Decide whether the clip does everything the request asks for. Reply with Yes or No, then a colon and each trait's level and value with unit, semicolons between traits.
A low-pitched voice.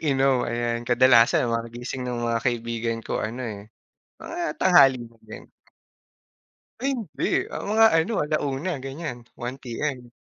Yes: low, 125 Hz